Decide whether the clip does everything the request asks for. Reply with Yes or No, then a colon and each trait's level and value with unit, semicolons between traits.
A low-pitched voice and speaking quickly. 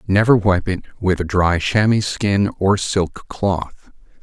No: very low, 95 Hz; average, 155 wpm